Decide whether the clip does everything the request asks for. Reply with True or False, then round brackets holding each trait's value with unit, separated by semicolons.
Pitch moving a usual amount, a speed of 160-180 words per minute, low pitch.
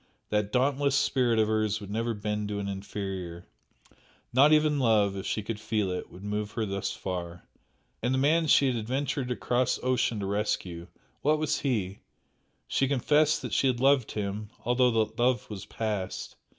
True (4.2 semitones; 175 wpm; 110 Hz)